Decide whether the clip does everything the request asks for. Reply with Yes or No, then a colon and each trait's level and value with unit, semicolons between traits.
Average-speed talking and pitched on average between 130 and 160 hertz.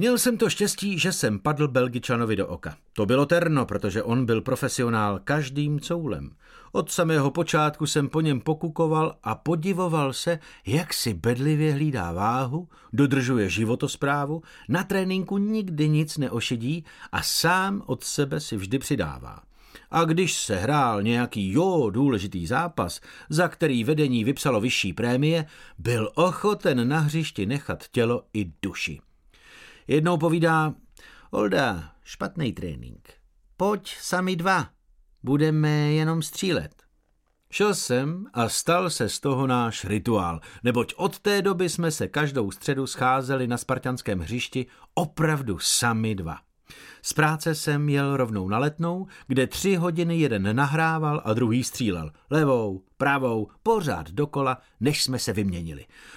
Yes: average, 135 wpm; medium, 140 Hz